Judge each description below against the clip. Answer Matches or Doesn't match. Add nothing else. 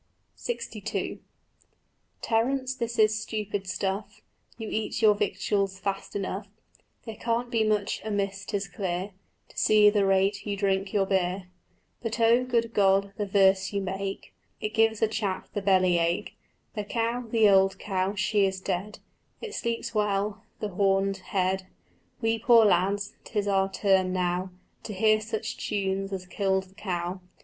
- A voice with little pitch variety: Matches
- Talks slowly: Doesn't match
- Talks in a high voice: Matches